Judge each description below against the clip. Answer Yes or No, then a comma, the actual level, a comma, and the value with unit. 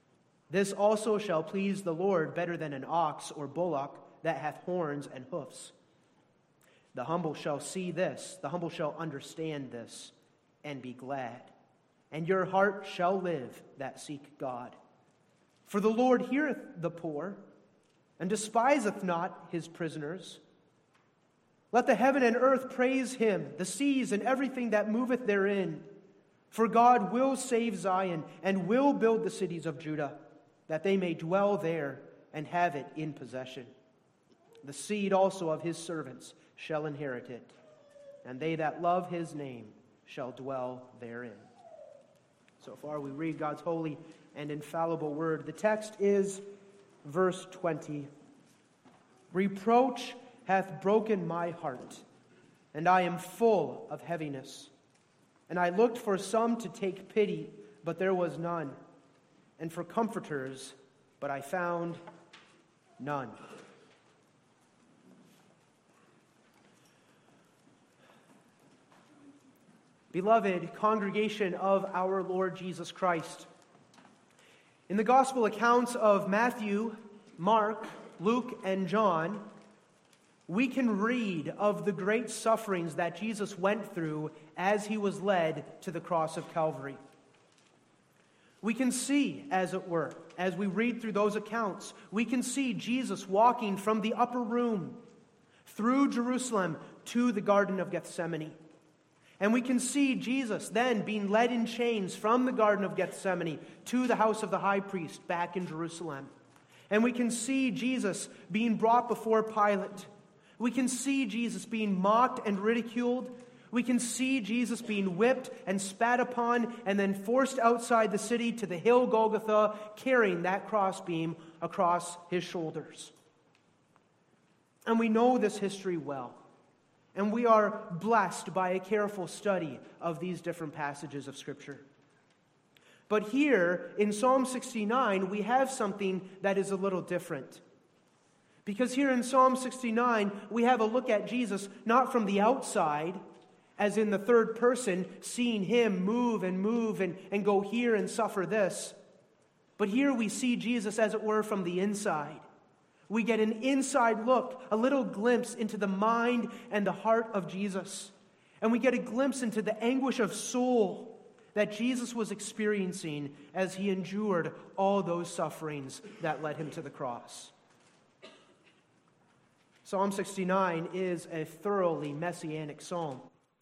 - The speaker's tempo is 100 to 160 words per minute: Yes, average, 140 wpm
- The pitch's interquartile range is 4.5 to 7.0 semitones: Yes, average, 5.3 semitones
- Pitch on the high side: Yes, high, 195 Hz